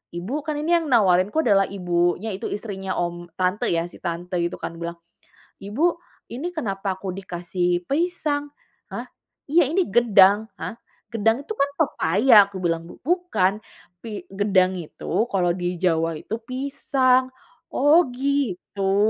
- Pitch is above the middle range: Yes, high, 200 Hz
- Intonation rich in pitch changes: Yes, wide, 7.1 semitones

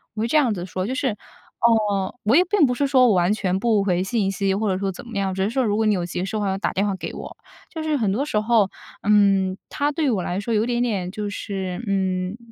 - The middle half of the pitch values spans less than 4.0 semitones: Yes, average, 3.6 semitones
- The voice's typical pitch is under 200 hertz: No, high, 205 Hz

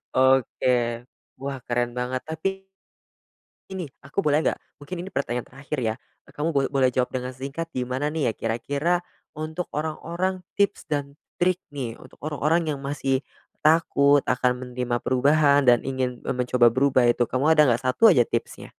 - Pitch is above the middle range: No, medium, 140 Hz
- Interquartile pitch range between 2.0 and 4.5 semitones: Yes, average, 3.5 semitones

